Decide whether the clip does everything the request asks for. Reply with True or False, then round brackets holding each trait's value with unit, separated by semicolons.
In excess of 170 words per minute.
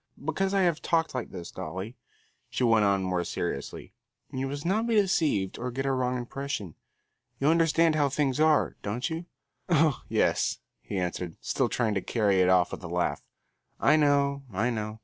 True (185 wpm)